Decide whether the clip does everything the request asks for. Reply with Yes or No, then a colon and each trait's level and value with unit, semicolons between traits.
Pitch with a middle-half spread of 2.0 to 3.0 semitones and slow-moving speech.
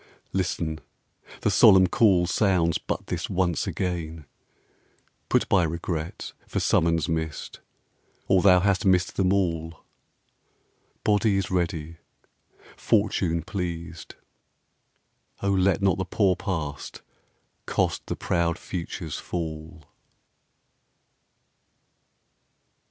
Yes: narrow, 2.5 semitones; slow, 95 wpm